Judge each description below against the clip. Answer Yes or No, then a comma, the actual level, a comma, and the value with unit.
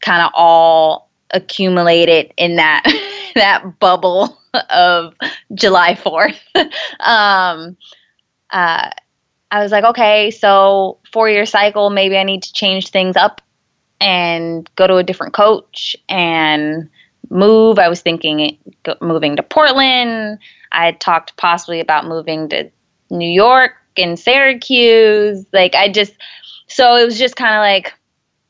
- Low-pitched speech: No, high, 195 Hz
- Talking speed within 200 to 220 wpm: No, slow, 135 wpm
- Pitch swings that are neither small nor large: Yes, average, 4.6 semitones